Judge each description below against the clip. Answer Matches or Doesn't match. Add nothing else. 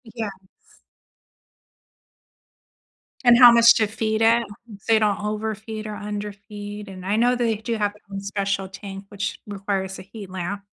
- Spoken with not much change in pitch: Matches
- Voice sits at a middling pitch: Doesn't match